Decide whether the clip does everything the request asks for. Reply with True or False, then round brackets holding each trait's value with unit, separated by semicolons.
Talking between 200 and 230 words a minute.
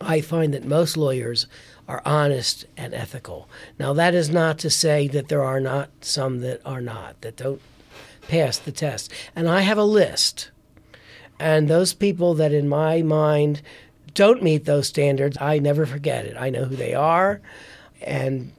False (175 wpm)